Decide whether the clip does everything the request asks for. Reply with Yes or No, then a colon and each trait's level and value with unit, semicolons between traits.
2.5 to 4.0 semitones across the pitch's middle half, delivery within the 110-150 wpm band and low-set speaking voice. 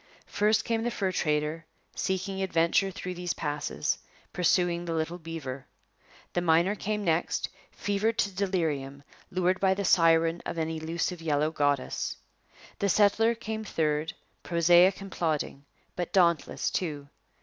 No: average, 3.4 semitones; average, 140 wpm; medium, 175 Hz